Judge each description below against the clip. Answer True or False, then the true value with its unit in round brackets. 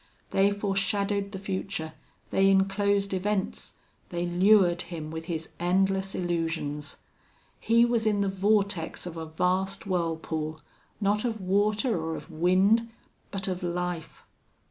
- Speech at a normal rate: False (130 wpm)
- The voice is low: False (190 Hz)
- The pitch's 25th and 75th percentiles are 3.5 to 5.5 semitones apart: False (2.8 semitones)